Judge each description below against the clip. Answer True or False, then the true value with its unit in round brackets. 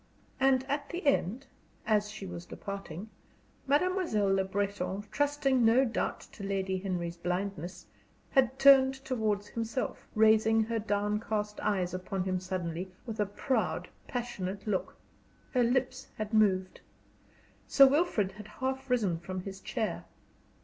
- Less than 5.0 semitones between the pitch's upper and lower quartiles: False (5.3 semitones)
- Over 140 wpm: False (135 wpm)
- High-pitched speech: True (210 Hz)